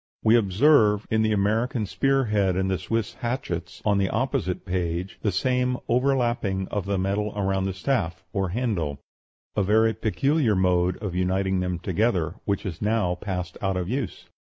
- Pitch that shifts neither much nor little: Yes, average, 3.7 semitones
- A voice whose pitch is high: No, low, 100 Hz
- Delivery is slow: No, average, 170 wpm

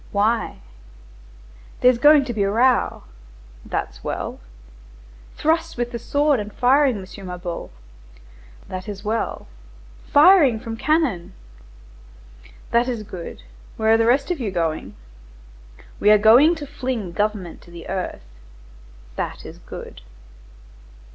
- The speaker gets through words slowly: Yes, slow, 130 wpm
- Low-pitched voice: No, high, 225 Hz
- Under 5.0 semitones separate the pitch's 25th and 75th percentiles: No, wide, 5.4 semitones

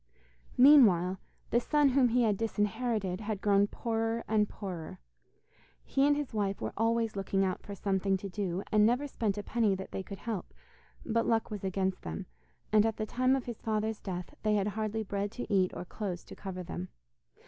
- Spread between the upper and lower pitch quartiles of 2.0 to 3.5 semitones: Yes, average, 2.9 semitones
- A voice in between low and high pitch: No, high, 210 Hz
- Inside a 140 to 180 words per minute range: No, average, 195 wpm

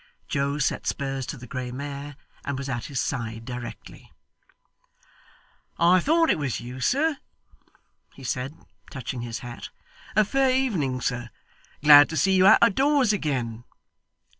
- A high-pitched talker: No, medium, 140 Hz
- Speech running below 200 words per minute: Yes, average, 150 wpm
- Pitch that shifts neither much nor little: No, wide, 7.3 semitones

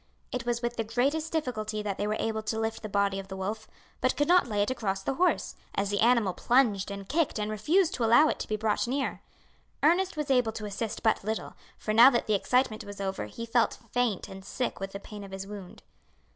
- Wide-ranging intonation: No, average, 3.6 semitones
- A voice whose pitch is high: Yes, high, 220 Hz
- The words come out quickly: Yes, fast, 240 wpm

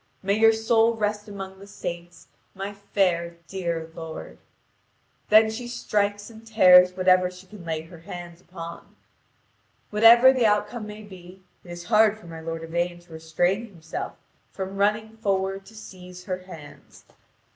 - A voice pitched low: No, high, 190 Hz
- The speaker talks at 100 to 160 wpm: Yes, average, 155 wpm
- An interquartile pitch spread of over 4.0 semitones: No, average, 3.4 semitones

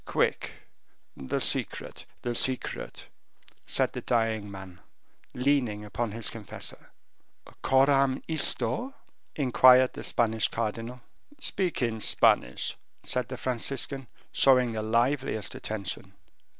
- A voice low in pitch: Yes, low, 120 Hz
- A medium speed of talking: No, slow, 105 wpm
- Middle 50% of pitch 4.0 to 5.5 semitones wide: No, average, 3.2 semitones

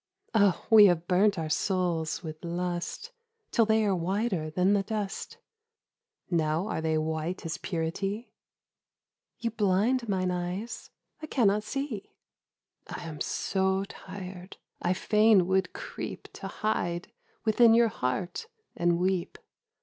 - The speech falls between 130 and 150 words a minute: Yes, average, 145 wpm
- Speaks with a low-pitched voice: No, high, 190 Hz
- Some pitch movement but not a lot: Yes, average, 3.6 semitones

